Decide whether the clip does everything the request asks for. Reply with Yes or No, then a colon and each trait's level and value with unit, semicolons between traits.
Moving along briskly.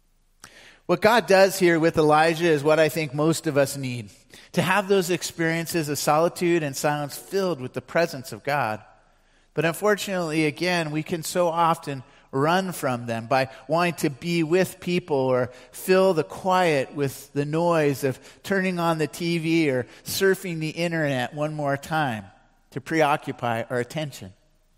No: average, 160 wpm